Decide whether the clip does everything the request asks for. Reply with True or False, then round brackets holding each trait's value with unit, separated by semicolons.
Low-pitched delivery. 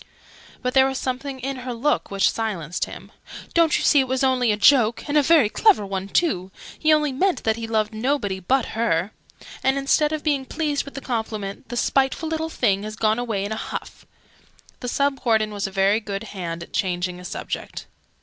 False (240 Hz)